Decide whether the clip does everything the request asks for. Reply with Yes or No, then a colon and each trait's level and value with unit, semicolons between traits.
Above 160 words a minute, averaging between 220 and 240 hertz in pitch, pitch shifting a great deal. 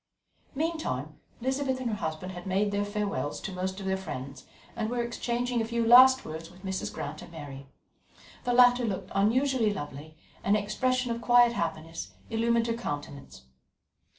No: average, 170 wpm; high, 205 Hz; wide, 6.7 semitones